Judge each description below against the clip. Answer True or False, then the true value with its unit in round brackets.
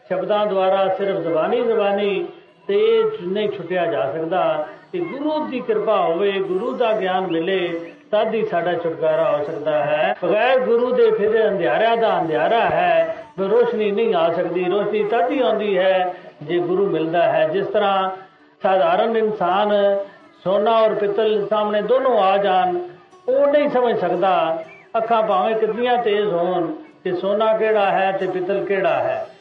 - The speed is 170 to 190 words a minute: False (150 wpm)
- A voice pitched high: True (210 Hz)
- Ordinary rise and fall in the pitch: True (4.6 semitones)